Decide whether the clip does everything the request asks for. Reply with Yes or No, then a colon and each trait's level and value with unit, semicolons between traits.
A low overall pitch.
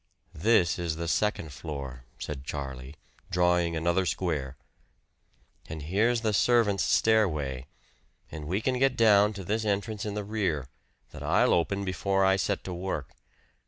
Yes: very low, 90 Hz